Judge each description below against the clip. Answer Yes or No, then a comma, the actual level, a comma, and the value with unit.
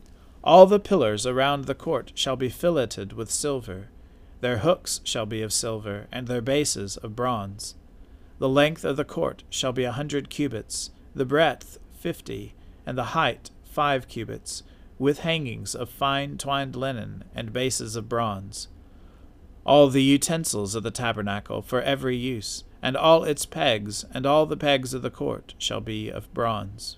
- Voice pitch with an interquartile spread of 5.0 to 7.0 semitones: Yes, wide, 5.6 semitones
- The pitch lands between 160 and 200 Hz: No, low, 120 Hz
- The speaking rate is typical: Yes, average, 165 wpm